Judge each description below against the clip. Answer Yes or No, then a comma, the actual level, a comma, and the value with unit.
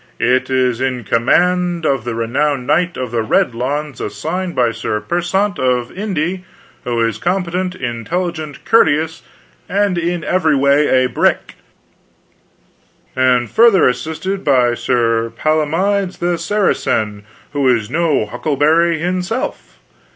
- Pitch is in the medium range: Yes, medium, 150 Hz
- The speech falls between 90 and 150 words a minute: Yes, slow, 135 wpm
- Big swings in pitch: Yes, wide, 6.2 semitones